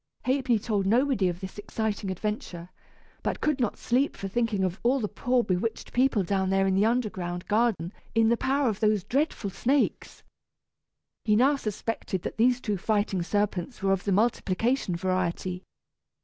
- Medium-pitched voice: No, high, 210 Hz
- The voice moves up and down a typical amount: Yes, average, 4.2 semitones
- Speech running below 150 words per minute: No, average, 165 wpm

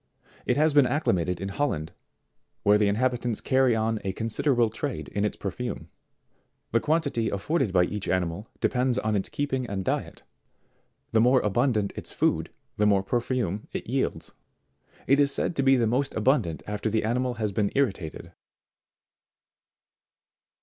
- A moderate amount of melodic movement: Yes, average, 4.5 semitones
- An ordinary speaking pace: Yes, average, 155 wpm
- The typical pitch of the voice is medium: No, low, 115 Hz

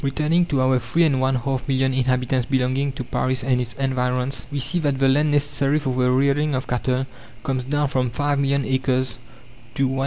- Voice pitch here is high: No, low, 130 Hz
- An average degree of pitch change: No, narrow, 1.6 semitones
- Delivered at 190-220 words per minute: Yes, fast, 205 wpm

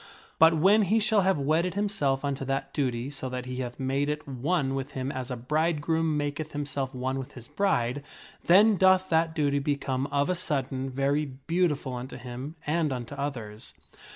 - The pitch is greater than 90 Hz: Yes, medium, 140 Hz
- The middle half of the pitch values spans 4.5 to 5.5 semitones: No, average, 3.6 semitones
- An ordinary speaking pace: Yes, average, 180 wpm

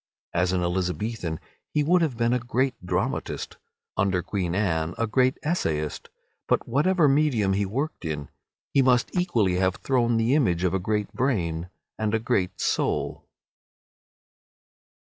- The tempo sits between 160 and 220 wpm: No, average, 145 wpm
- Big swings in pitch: Yes, wide, 6.3 semitones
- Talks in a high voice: No, low, 110 Hz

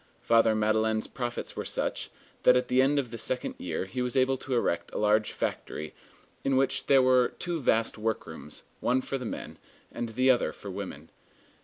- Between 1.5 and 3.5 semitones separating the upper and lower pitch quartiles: Yes, average, 3.2 semitones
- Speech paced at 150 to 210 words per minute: Yes, average, 190 wpm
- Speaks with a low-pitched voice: Yes, low, 120 Hz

